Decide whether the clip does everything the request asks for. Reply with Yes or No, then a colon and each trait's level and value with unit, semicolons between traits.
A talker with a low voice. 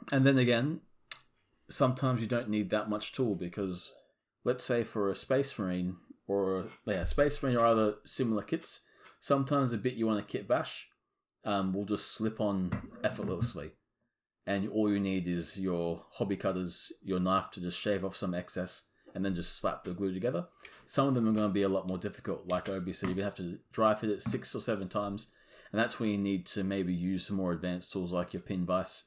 Yes: low, 100 Hz